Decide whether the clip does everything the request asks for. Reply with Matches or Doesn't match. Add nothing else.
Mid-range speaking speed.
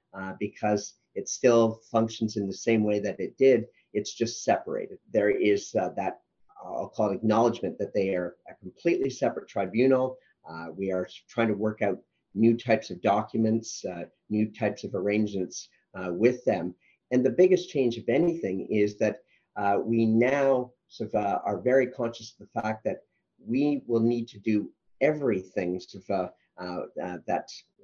Matches